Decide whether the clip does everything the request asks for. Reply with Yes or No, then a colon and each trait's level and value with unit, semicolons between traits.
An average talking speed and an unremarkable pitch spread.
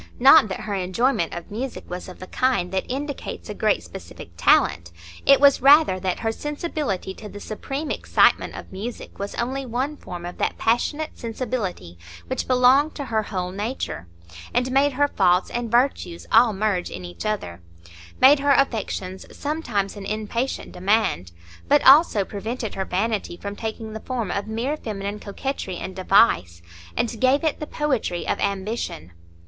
No: average, 165 wpm; wide, 5.7 semitones